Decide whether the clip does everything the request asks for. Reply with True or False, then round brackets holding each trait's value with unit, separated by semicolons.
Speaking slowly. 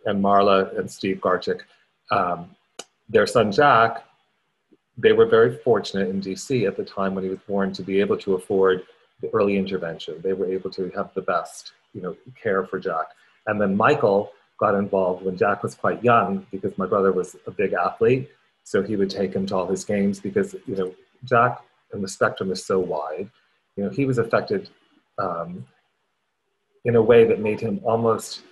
False (195 wpm)